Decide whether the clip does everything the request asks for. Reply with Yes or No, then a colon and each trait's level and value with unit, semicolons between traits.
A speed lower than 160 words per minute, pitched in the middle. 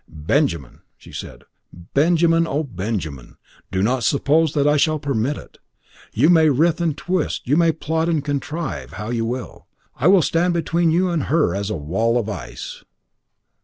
No: average, 170 wpm; medium, 145 Hz